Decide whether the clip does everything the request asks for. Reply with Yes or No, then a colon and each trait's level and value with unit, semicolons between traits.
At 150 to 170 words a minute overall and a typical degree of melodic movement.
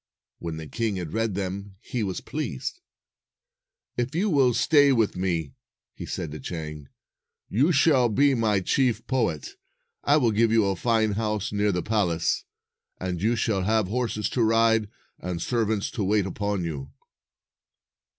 Yes: average, 160 wpm; average, 4.6 semitones